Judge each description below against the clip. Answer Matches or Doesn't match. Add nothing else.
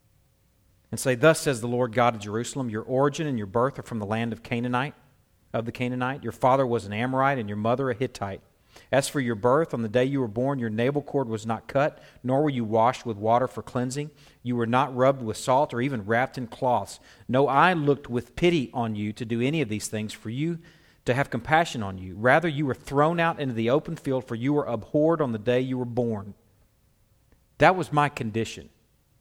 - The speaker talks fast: Matches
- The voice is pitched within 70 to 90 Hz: Doesn't match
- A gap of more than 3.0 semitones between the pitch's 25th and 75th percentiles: Matches